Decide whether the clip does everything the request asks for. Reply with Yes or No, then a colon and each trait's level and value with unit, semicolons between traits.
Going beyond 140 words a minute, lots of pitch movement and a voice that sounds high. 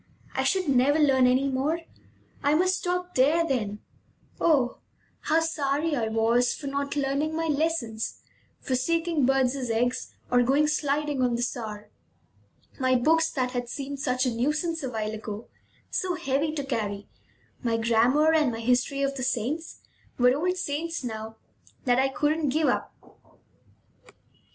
No: average, 155 wpm; average, 3.9 semitones; very high, 275 Hz